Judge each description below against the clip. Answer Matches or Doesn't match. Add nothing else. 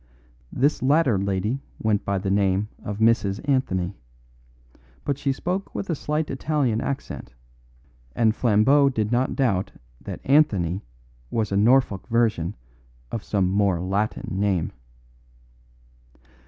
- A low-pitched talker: Matches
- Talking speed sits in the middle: Doesn't match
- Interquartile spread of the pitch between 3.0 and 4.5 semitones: Doesn't match